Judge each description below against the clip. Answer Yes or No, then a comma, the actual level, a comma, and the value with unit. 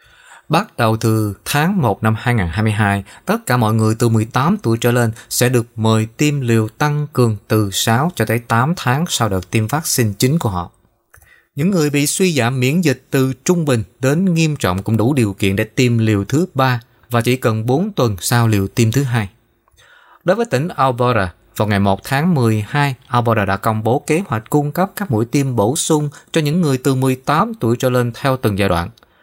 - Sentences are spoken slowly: No, average, 210 wpm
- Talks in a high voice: No, low, 125 Hz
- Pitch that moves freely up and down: No, average, 4.8 semitones